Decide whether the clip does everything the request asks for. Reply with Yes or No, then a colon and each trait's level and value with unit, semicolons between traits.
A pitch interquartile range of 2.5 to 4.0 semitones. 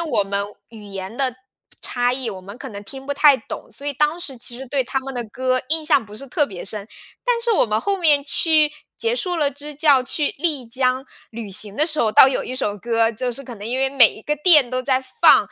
No: average, 4.5 semitones